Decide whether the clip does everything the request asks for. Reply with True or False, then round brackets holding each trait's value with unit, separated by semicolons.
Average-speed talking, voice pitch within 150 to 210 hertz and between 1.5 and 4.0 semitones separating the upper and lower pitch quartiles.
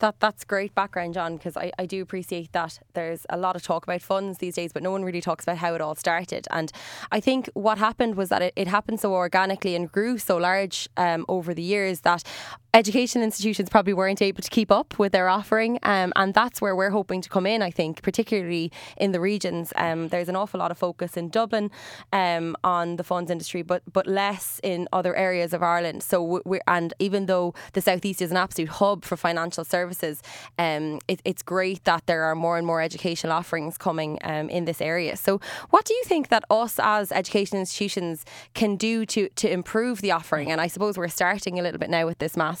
False (225 wpm; 185 Hz; 2.8 semitones)